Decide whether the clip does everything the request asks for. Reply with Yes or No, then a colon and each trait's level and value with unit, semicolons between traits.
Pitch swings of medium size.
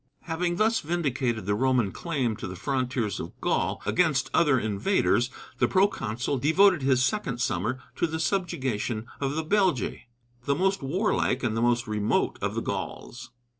No: wide, 6.3 semitones